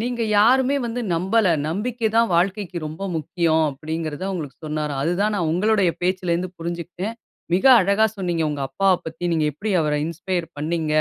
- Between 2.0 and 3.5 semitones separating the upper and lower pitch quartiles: No, average, 4.2 semitones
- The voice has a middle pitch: Yes, medium, 175 Hz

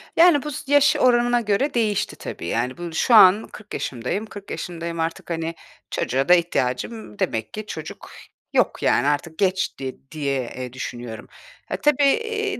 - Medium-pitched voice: Yes, medium, 180 Hz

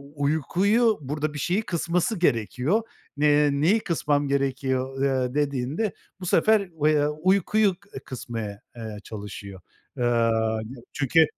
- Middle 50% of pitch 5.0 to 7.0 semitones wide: Yes, average, 5.3 semitones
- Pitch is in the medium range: Yes, medium, 145 Hz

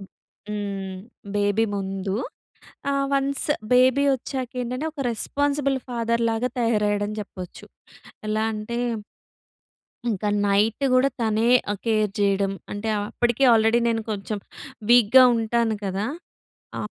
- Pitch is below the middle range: No, high, 225 Hz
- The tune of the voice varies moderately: Yes, average, 3.1 semitones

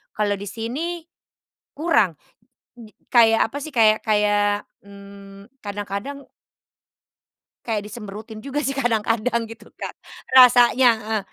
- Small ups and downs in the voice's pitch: No, average, 3.1 semitones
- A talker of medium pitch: No, high, 220 Hz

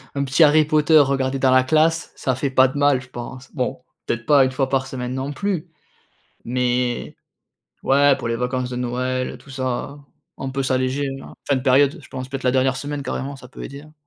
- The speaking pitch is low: Yes, low, 130 Hz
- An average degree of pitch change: No, narrow, 1.9 semitones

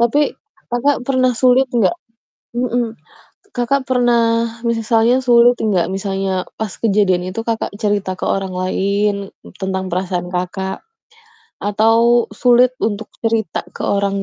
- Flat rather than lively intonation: No, average, 3.8 semitones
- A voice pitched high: Yes, high, 225 Hz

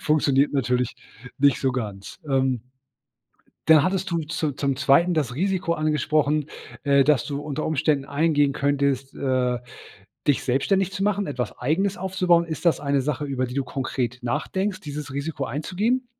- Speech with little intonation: No, average, 3.7 semitones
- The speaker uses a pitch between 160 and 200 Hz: No, medium, 145 Hz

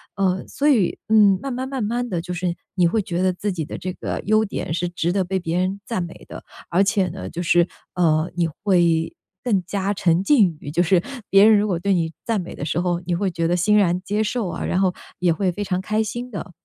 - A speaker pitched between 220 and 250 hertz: No, medium, 185 Hz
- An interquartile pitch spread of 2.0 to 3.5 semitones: Yes, average, 2.9 semitones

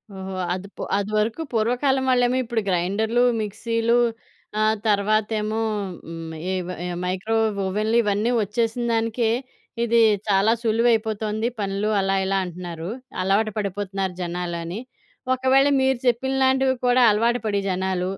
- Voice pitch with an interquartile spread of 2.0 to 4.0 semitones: Yes, average, 3.4 semitones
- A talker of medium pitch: No, high, 215 Hz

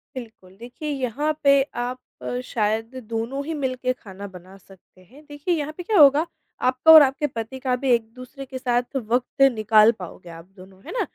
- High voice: Yes, very high, 250 Hz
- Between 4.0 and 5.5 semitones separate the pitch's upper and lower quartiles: Yes, average, 4.3 semitones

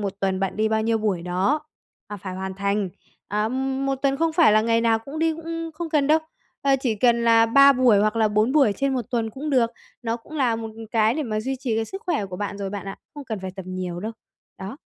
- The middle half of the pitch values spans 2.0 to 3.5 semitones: No, average, 4.9 semitones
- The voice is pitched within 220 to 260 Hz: Yes, high, 225 Hz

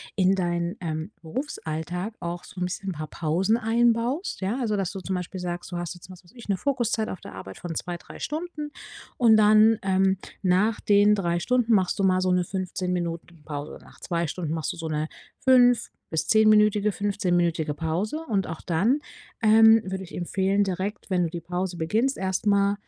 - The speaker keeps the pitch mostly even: No, average, 3.8 semitones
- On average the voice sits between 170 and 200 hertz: Yes, high, 190 Hz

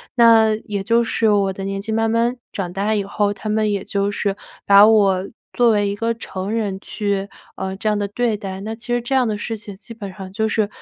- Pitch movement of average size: No, narrow, 2.2 semitones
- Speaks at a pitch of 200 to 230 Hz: Yes, high, 210 Hz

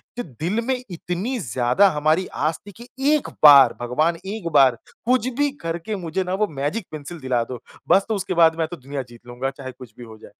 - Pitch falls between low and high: Yes, medium, 160 Hz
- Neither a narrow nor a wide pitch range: No, wide, 6.4 semitones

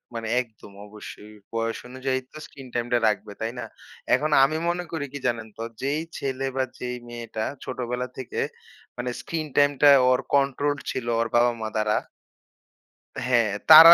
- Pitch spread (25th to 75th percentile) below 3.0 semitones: No, average, 3.5 semitones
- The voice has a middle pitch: No, low, 125 Hz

